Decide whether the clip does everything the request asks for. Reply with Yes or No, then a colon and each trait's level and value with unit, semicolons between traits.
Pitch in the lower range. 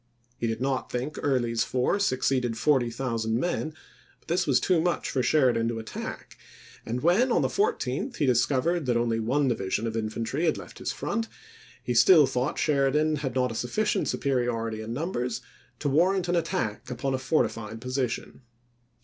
Yes: low, 130 Hz